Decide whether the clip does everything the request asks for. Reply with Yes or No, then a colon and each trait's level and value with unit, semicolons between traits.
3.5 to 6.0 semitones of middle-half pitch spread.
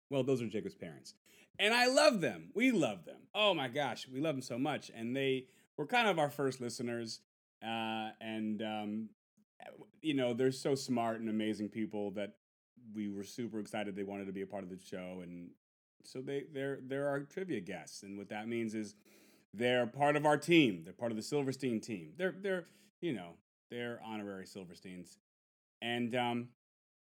Yes: average, 4.7 semitones